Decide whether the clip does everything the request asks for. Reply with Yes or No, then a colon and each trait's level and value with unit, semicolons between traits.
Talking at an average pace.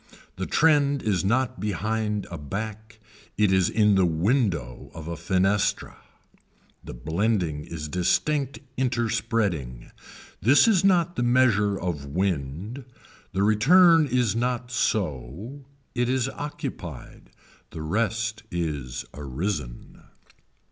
No: slow, 115 wpm